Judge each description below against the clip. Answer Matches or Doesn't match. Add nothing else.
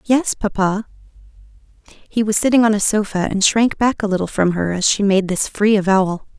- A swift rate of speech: Doesn't match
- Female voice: Matches